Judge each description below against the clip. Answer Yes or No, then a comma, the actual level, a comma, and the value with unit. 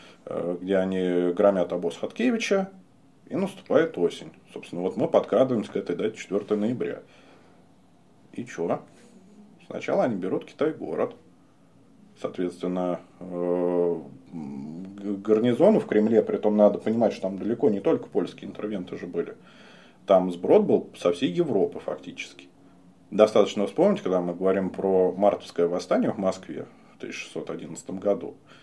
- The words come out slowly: No, average, 125 wpm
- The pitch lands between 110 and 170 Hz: No, very low, 95 Hz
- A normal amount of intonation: Yes, average, 3.1 semitones